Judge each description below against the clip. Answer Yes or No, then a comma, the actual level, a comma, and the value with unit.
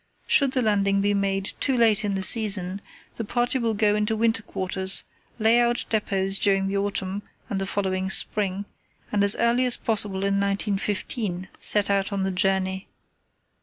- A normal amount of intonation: No, narrow, 2.3 semitones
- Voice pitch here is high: Yes, high, 200 Hz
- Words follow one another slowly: No, average, 170 wpm